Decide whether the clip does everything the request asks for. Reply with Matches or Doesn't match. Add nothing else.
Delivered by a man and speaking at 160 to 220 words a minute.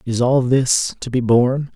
Matches